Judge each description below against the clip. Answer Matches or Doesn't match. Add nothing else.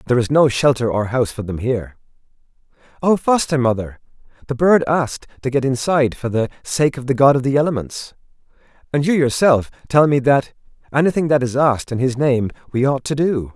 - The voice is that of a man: Matches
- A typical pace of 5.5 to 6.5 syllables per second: Matches